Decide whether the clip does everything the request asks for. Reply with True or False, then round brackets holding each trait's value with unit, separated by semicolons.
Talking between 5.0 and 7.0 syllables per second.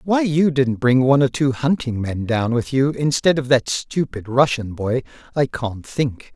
False (4.4 syllables/s)